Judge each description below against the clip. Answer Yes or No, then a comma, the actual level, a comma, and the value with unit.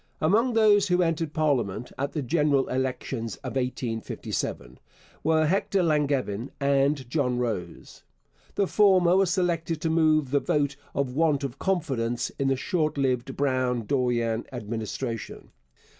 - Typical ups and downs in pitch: Yes, average, 4.6 semitones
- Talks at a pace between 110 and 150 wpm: Yes, average, 140 wpm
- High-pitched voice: No, medium, 140 Hz